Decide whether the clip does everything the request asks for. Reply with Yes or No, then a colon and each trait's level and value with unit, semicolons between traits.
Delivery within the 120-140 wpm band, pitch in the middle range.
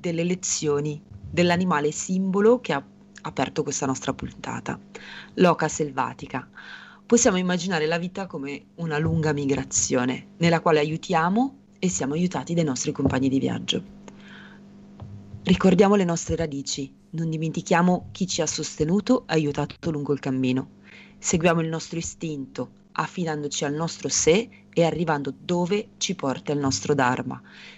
Yes: average, 135 wpm; medium, 165 Hz